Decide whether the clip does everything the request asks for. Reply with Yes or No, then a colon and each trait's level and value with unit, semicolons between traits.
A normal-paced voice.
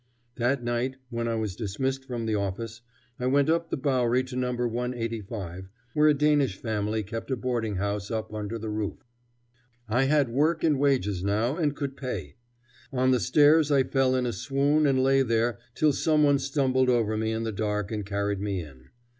Yes: average, 195 wpm